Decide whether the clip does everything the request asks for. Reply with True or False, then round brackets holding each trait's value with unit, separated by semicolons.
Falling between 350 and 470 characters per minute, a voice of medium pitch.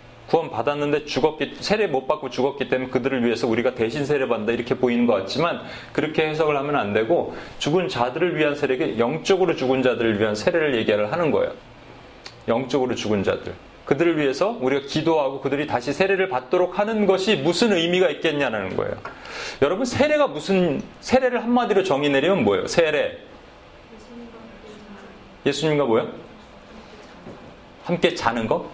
True (365 characters per minute; 150 Hz)